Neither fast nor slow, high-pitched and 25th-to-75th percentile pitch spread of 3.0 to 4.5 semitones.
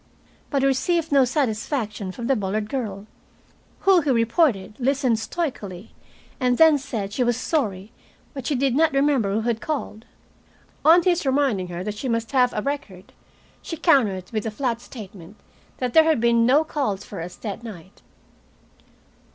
No: average, 170 wpm; high, 240 Hz; average, 5.1 semitones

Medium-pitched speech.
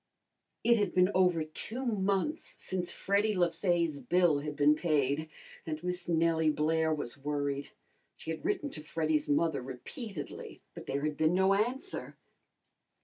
Yes: medium, 165 Hz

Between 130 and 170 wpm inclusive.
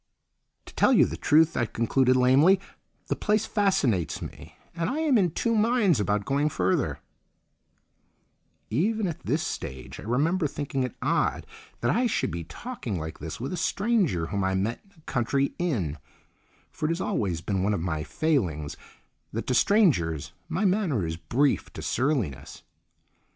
Yes: average, 165 wpm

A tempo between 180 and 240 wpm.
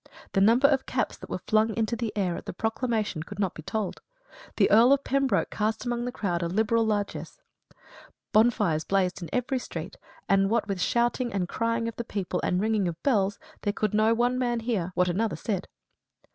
Yes: average, 200 wpm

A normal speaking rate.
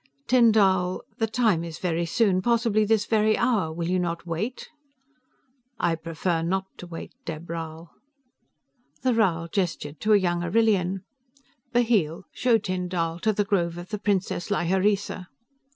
Yes: average, 150 wpm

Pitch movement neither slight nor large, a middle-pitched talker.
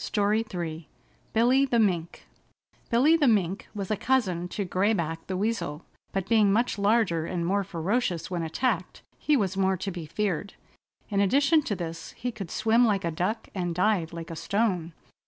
No: average, 4.6 semitones; high, 195 Hz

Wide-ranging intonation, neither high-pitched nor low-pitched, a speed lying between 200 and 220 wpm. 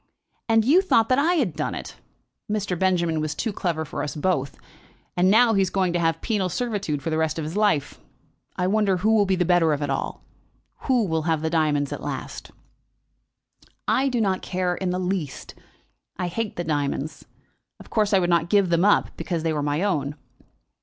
No: average, 4.6 semitones; medium, 180 Hz; fast, 205 wpm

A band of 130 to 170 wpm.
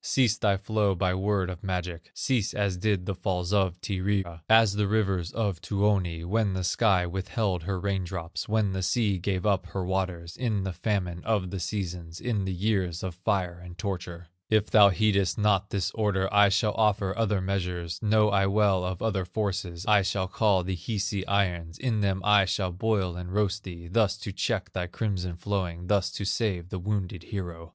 No: average, 190 wpm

